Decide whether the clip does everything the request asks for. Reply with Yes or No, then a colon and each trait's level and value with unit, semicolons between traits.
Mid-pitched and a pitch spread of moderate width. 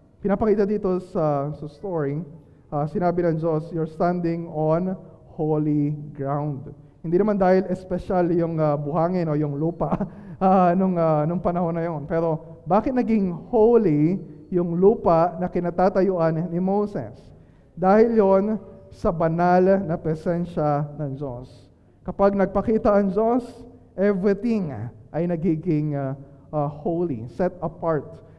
Yes: medium, 170 Hz; average, 3.9 semitones